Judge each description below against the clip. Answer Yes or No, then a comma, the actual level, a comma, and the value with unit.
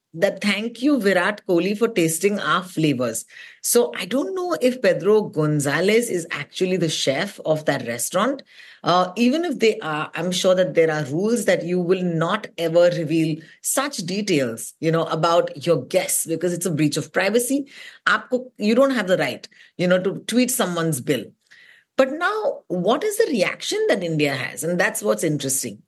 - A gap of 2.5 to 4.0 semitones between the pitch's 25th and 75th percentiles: No, wide, 5.5 semitones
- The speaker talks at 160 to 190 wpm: Yes, average, 180 wpm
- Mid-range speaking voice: Yes, medium, 180 Hz